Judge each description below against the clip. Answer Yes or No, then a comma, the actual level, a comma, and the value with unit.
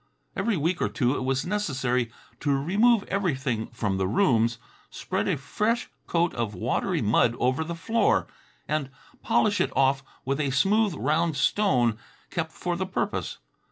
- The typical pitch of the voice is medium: Yes, medium, 145 Hz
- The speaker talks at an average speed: Yes, average, 155 wpm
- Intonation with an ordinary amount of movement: No, wide, 6.8 semitones